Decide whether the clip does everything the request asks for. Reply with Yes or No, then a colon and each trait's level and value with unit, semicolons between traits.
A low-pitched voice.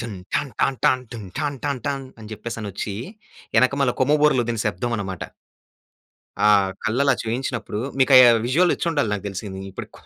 Yes: low, 120 Hz